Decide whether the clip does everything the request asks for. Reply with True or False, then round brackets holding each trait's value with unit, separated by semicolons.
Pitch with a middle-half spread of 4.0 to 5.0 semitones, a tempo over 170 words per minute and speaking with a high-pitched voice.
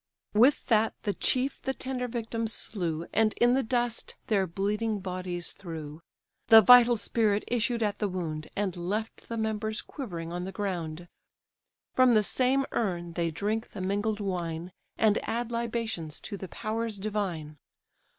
False (4.4 semitones; 155 wpm; 210 Hz)